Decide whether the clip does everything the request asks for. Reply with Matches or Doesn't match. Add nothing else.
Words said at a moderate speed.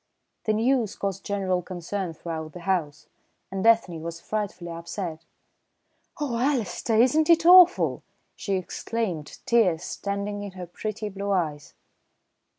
Doesn't match